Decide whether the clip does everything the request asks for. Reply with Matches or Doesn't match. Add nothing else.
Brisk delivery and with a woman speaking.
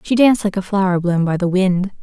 Matches